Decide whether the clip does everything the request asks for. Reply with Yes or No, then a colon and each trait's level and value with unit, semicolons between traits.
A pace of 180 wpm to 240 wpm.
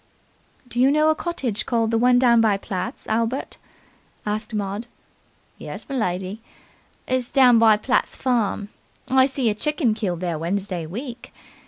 No: average, 150 wpm